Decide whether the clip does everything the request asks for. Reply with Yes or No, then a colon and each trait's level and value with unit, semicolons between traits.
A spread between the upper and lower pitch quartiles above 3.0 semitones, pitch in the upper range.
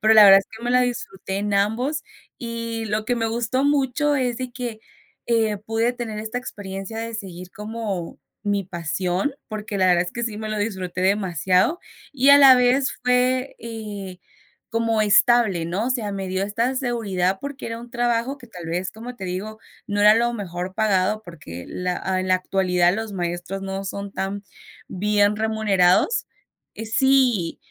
Yes: average, 3.9 semitones; high, 215 Hz